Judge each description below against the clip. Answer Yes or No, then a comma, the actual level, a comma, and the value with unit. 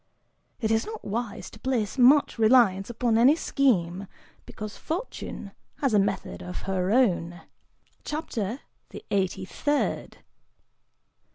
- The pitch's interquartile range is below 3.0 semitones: No, average, 5.2 semitones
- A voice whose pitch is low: No, high, 225 Hz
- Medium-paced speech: No, slow, 120 wpm